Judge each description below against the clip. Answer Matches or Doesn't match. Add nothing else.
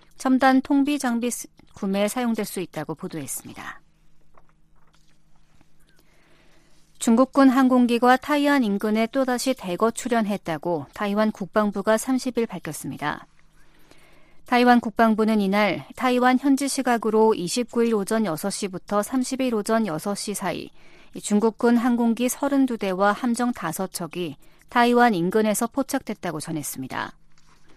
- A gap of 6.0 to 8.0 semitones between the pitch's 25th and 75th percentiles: Doesn't match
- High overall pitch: Matches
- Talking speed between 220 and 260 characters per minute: Matches